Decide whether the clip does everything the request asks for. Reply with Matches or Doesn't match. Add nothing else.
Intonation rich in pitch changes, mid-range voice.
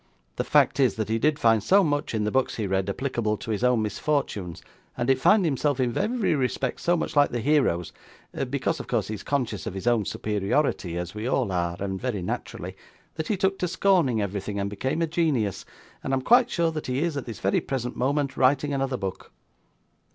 Doesn't match